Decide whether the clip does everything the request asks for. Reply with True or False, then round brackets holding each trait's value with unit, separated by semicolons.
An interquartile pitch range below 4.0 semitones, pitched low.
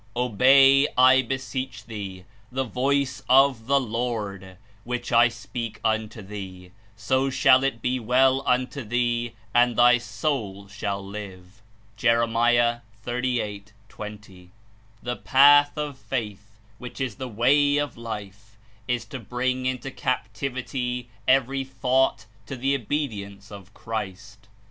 True (3.5 semitones; 120 Hz)